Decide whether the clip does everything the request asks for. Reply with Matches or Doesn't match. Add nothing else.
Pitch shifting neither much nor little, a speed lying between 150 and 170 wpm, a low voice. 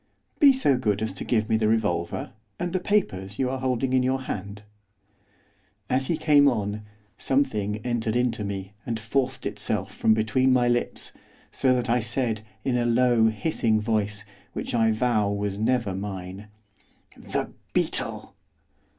Matches